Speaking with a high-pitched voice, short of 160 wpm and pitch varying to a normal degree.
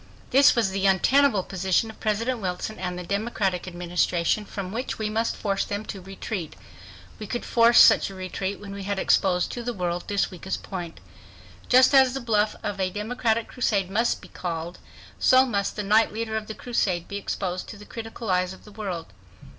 No: high, 200 Hz; average, 195 wpm; average, 3.3 semitones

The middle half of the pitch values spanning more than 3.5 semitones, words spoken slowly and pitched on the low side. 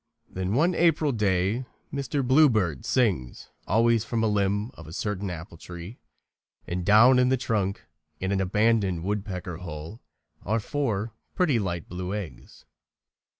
No: average, 4.5 semitones; average, 145 wpm; low, 105 Hz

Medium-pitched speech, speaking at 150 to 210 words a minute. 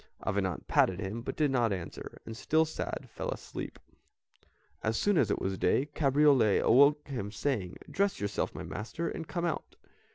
No: low, 125 Hz; average, 170 wpm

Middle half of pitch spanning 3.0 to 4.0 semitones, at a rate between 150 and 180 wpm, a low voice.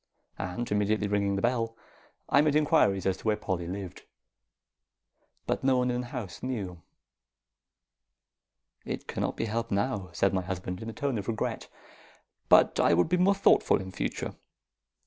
No: average, 4.6 semitones; average, 165 wpm; low, 105 Hz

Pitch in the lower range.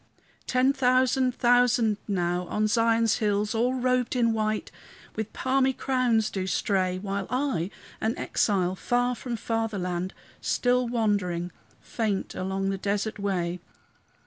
No: high, 220 Hz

